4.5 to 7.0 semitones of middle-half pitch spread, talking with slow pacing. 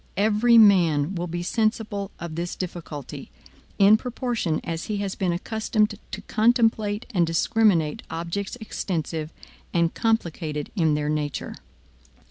Yes: average, 4.8 semitones; slow, 125 wpm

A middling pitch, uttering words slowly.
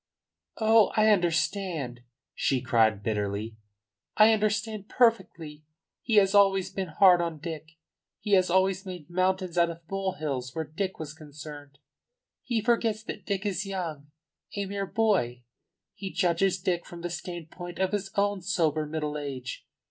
No: medium, 180 Hz; average, 150 wpm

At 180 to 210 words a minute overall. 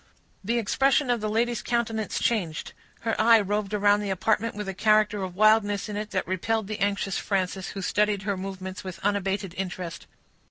Yes: average, 185 wpm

